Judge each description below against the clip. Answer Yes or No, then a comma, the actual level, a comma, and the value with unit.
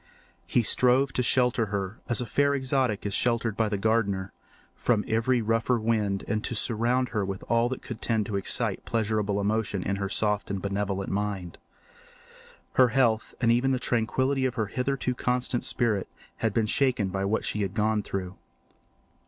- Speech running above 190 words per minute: No, average, 175 wpm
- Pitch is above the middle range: No, low, 110 Hz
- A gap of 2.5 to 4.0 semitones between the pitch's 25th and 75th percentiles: Yes, average, 3.4 semitones